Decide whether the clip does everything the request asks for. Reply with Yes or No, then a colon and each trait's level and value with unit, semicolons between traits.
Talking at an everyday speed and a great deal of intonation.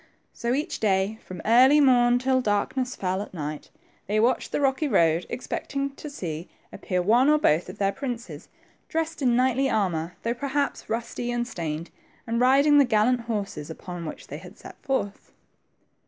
Yes: average, 170 wpm; wide, 5.7 semitones